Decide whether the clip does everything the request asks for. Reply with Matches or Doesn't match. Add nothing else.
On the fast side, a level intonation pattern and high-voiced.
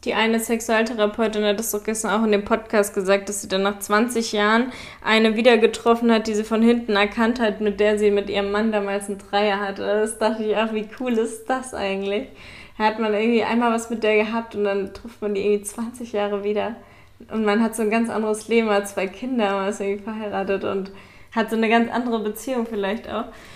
Matches